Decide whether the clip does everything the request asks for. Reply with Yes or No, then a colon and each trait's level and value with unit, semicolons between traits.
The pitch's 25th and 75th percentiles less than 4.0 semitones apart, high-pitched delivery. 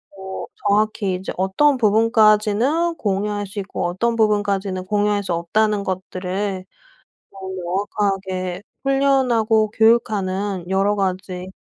Yes: narrow, 2.4 semitones; high, 205 Hz